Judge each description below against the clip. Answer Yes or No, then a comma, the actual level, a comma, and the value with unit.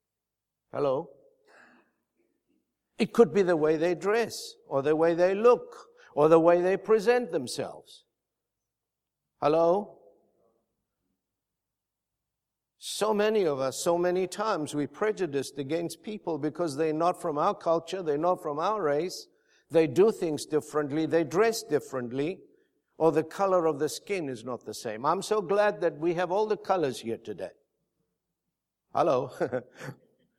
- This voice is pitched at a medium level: Yes, medium, 165 Hz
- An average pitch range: No, wide, 6.5 semitones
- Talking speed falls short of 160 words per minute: Yes, average, 140 wpm